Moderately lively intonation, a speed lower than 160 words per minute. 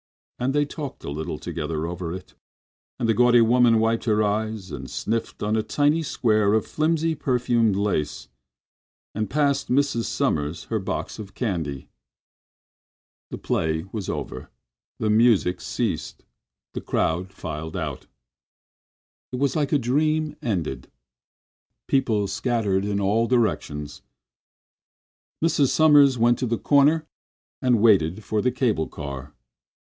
No: wide, 5.7 semitones; slow, 135 wpm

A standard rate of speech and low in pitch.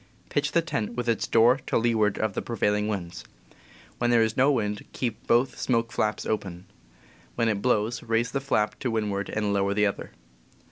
Yes: average, 190 wpm; low, 110 Hz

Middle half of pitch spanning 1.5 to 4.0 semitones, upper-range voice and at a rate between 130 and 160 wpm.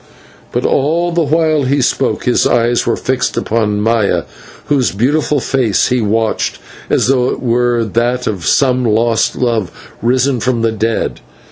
No: average, 2.8 semitones; low, 120 Hz; average, 155 wpm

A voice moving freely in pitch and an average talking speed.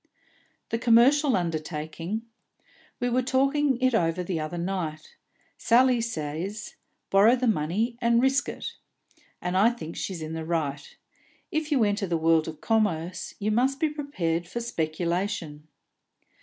Yes: wide, 6.7 semitones; average, 145 wpm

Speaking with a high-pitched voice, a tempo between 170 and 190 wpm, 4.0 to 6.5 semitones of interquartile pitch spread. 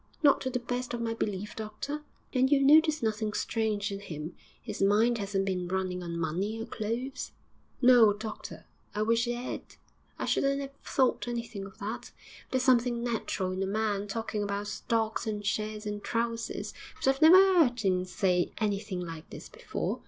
No: high, 220 Hz; average, 180 wpm; average, 3.3 semitones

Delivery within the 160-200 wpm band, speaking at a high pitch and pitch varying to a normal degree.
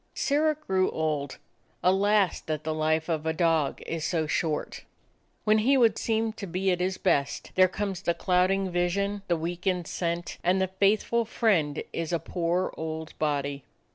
No: average, 170 wpm; medium, 180 Hz; average, 3.8 semitones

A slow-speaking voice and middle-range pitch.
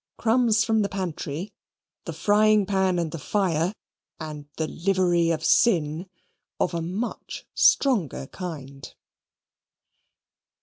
Yes: slow, 115 wpm; medium, 180 Hz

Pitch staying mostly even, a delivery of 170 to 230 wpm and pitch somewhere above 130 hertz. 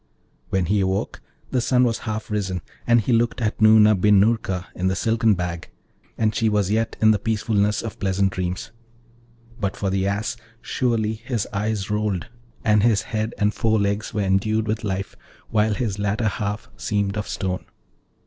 No: narrow, 2.1 semitones; average, 175 wpm; low, 105 Hz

